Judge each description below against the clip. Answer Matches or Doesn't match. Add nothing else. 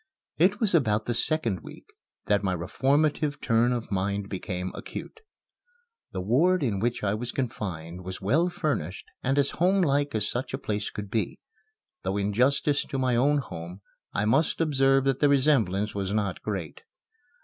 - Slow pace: Doesn't match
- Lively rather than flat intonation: Matches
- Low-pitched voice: Matches